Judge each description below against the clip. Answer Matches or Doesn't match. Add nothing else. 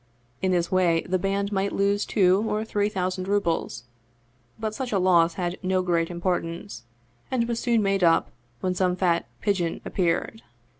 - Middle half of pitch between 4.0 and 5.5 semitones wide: Doesn't match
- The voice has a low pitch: Doesn't match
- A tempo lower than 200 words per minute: Matches